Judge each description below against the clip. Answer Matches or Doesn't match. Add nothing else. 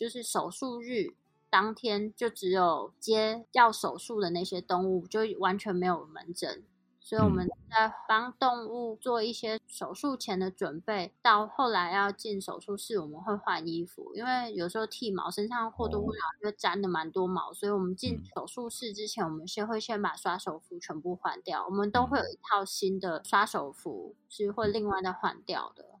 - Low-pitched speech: Doesn't match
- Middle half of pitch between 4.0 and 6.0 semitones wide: Doesn't match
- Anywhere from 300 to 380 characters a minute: Doesn't match